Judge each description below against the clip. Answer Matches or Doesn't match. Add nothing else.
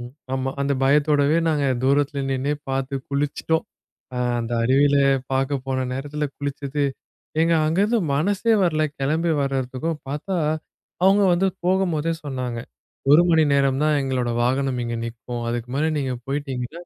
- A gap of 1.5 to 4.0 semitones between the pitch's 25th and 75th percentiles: Matches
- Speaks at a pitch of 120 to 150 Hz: Matches